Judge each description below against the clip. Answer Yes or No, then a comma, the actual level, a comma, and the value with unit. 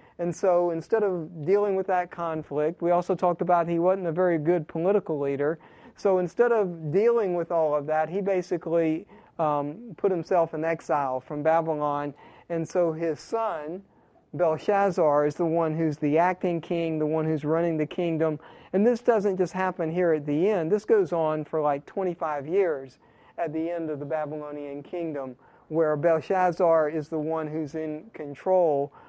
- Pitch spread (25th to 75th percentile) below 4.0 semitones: Yes, average, 2.9 semitones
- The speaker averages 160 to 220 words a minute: Yes, average, 175 wpm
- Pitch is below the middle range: No, medium, 165 Hz